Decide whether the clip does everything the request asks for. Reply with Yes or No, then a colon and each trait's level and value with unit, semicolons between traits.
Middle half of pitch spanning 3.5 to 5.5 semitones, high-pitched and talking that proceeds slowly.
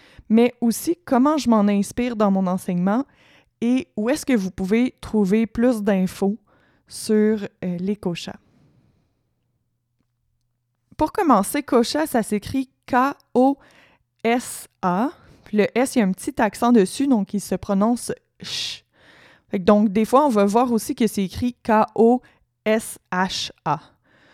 Yes: average, 3.9 semitones; high, 220 Hz; slow, 130 wpm